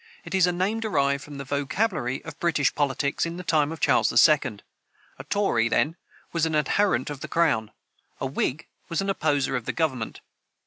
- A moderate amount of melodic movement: Yes, average, 4.1 semitones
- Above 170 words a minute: Yes, average, 190 wpm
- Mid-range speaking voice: Yes, medium, 150 Hz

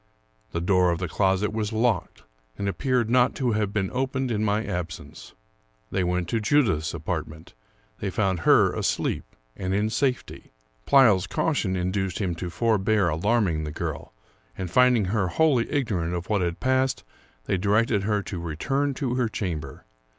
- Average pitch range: Yes, average, 4.9 semitones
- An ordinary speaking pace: Yes, average, 170 wpm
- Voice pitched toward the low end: Yes, low, 100 Hz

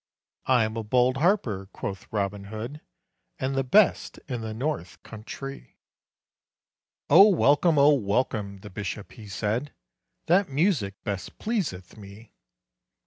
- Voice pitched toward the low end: Yes, low, 115 Hz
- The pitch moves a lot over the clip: Yes, wide, 5.9 semitones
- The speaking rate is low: Yes, slow, 130 wpm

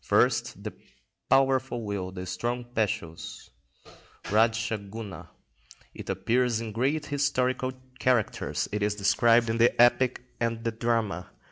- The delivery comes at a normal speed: No, slow, 125 wpm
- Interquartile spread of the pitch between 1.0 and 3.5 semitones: Yes, average, 2.9 semitones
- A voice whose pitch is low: Yes, low, 115 Hz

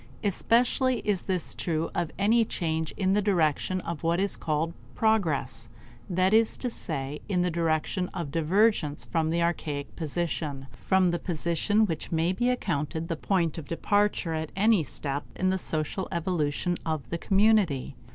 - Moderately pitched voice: Yes, medium, 170 Hz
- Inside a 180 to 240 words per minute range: No, average, 160 wpm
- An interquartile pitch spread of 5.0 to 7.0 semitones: No, average, 3.8 semitones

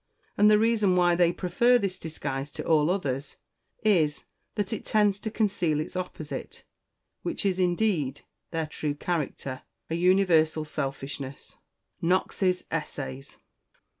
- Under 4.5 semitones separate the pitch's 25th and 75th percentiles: No, average, 4.8 semitones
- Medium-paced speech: No, slow, 130 wpm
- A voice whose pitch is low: No, medium, 175 Hz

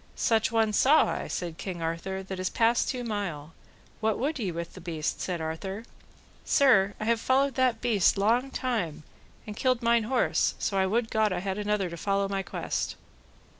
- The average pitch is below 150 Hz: No, high, 210 Hz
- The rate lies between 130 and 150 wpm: No, average, 185 wpm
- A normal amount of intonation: Yes, average, 4.1 semitones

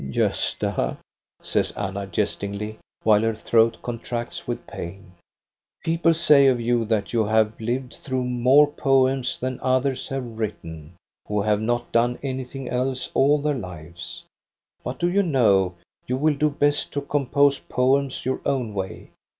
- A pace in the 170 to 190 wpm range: No, average, 150 wpm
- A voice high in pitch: No, low, 125 Hz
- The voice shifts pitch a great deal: No, average, 4.1 semitones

